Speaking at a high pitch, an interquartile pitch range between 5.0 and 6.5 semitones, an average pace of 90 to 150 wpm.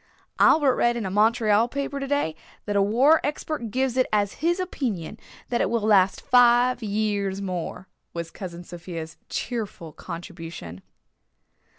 Yes: high, 215 Hz; wide, 5.4 semitones; average, 145 wpm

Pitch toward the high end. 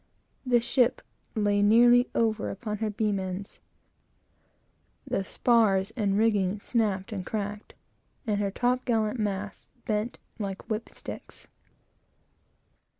Yes: high, 210 Hz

